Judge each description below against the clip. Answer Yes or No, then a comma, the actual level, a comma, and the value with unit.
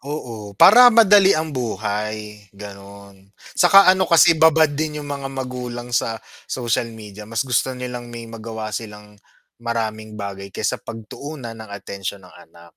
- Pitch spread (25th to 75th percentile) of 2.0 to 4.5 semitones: No, average, 5.0 semitones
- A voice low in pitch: Yes, low, 115 Hz